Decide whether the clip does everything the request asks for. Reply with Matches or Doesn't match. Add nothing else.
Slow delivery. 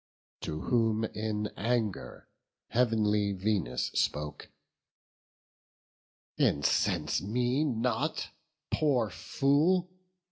Matches